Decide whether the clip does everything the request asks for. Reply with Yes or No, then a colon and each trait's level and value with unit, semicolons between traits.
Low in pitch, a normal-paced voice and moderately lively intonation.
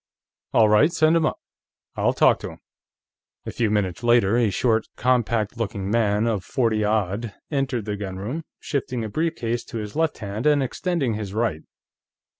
Yes: low, 115 Hz; average, 175 wpm; average, 3.6 semitones